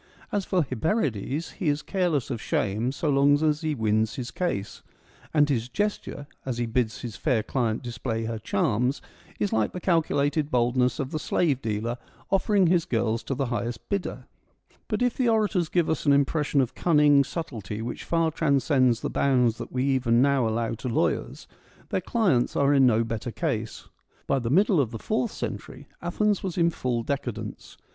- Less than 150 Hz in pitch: Yes, low, 135 Hz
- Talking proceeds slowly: No, average, 185 wpm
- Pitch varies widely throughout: Yes, wide, 5.7 semitones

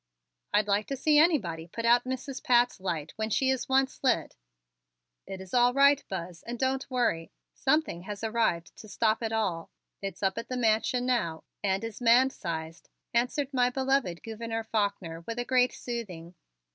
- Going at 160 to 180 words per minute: Yes, average, 170 wpm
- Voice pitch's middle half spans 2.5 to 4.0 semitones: No, average, 5.0 semitones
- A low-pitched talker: No, high, 230 Hz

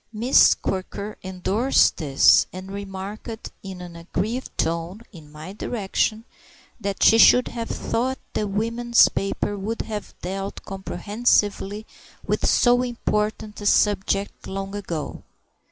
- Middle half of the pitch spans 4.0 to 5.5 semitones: No, average, 2.8 semitones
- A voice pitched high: Yes, high, 205 Hz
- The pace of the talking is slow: Yes, slow, 120 wpm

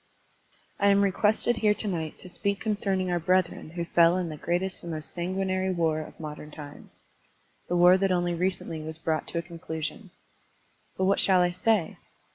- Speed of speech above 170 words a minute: Yes, average, 200 wpm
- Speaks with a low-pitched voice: No, medium, 175 Hz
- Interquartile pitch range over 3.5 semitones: No, narrow, 2.6 semitones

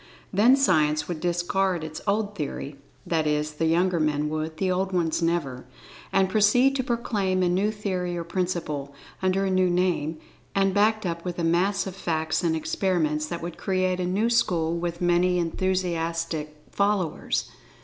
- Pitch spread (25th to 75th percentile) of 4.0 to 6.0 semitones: No, average, 3.0 semitones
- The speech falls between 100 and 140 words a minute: No, average, 165 wpm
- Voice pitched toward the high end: No, medium, 175 Hz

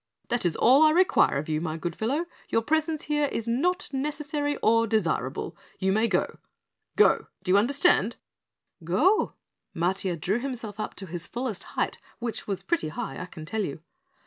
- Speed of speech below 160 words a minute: No, average, 175 wpm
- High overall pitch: Yes, high, 225 Hz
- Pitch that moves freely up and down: Yes, wide, 8.0 semitones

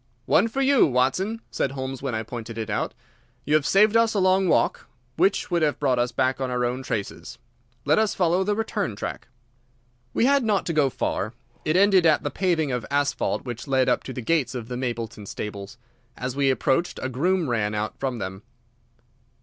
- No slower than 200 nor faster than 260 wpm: Yes, fast, 205 wpm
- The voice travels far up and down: Yes, wide, 7.2 semitones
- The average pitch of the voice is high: No, low, 135 Hz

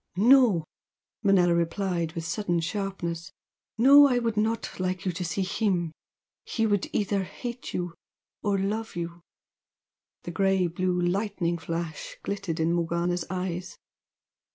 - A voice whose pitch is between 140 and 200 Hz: Yes, medium, 185 Hz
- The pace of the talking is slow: Yes, slow, 130 wpm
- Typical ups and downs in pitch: Yes, average, 3.1 semitones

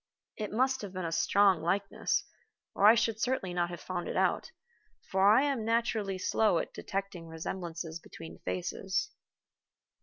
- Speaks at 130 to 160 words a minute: Yes, average, 155 wpm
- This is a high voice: Yes, high, 195 Hz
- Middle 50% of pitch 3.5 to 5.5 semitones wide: Yes, average, 4.3 semitones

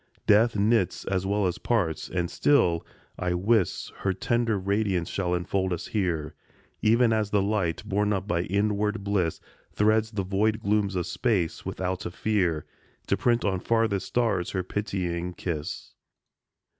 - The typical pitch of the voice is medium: No, low, 100 Hz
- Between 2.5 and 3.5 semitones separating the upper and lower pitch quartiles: Yes, average, 3.2 semitones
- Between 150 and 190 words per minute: Yes, average, 155 wpm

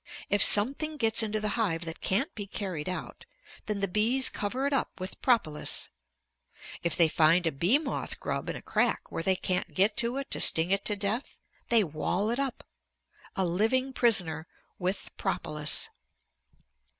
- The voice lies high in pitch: Yes, high, 205 Hz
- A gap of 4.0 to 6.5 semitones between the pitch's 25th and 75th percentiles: Yes, average, 5.1 semitones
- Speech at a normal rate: Yes, average, 175 wpm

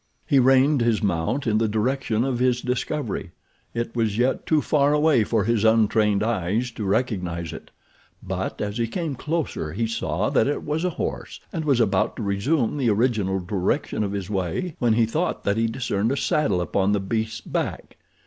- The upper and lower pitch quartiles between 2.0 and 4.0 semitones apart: No, average, 4.7 semitones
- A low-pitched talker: Yes, low, 115 Hz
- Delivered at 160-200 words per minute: Yes, average, 190 wpm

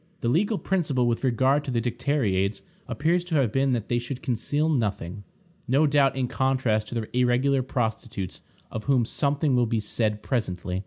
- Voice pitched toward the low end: Yes, low, 125 Hz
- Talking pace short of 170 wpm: No, average, 175 wpm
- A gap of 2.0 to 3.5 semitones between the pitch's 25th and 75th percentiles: No, average, 3.9 semitones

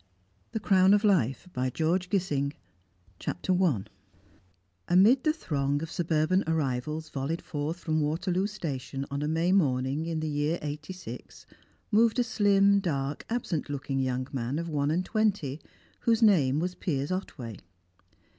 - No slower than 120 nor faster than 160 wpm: Yes, average, 145 wpm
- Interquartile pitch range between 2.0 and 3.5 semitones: No, average, 5.1 semitones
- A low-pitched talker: No, medium, 160 Hz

